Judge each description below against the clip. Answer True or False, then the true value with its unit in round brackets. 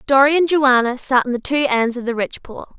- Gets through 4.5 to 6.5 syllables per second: True (5.9 syllables/s)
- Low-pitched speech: False (260 Hz)